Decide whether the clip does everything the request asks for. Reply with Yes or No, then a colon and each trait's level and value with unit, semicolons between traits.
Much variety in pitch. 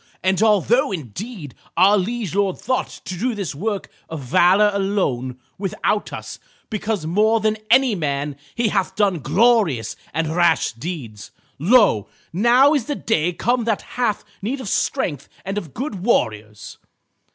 Yes: wide, 5.8 semitones